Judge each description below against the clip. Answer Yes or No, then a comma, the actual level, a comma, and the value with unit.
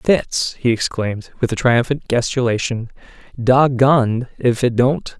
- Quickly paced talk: No, average, 140 wpm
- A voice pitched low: Yes, low, 125 Hz